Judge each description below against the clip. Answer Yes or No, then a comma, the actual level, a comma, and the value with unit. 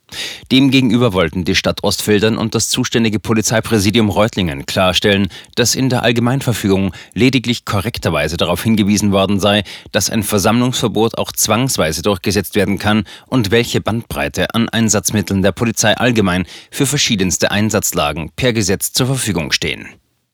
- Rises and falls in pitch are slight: No, average, 3.1 semitones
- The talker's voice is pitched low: Yes, low, 105 Hz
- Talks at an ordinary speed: Yes, average, 135 wpm